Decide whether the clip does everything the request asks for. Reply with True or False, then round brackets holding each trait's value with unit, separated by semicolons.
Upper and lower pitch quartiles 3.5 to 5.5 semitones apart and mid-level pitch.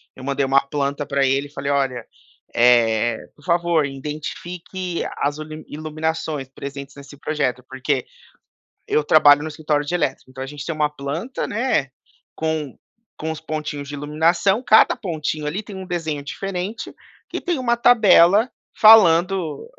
True (3.9 semitones; 150 Hz)